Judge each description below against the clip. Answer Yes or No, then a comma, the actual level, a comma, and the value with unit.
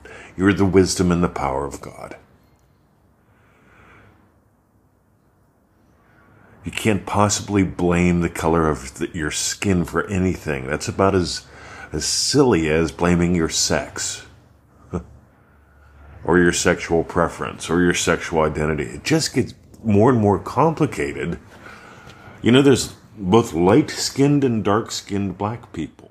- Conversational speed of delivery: No, slow, 120 wpm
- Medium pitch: No, very low, 95 Hz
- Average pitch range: Yes, average, 4.1 semitones